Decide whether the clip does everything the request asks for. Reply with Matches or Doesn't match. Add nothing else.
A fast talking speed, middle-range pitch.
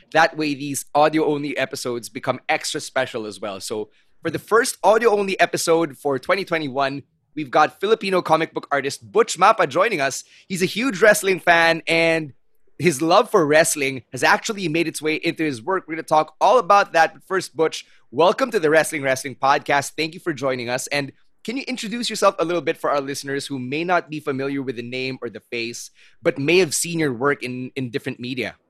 Matches